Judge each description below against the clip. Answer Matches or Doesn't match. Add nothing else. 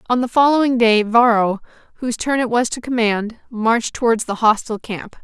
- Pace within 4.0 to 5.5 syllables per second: Matches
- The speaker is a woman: Matches